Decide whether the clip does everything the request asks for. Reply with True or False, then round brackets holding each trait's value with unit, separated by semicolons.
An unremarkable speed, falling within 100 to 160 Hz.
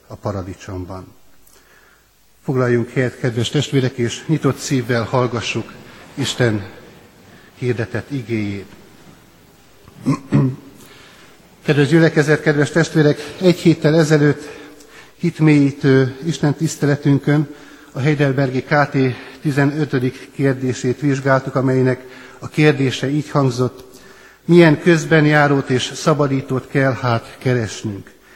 False (90 wpm; 135 Hz)